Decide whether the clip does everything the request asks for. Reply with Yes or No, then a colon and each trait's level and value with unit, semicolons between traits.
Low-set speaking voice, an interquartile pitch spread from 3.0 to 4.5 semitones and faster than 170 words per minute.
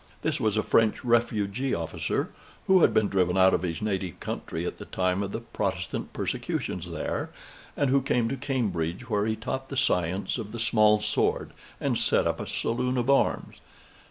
No: low, 110 Hz; average, 4.9 semitones; average, 185 wpm